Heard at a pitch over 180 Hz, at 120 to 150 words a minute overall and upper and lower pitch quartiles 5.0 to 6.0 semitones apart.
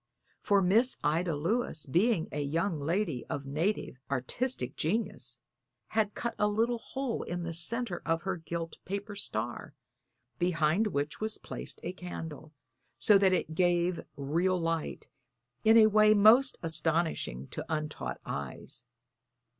No: medium, 175 Hz; average, 140 wpm; average, 5.3 semitones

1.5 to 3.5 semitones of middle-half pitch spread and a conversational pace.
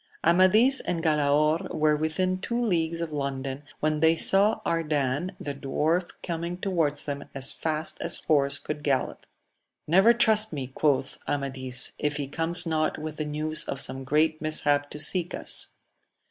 Yes: average, 2.9 semitones; average, 160 wpm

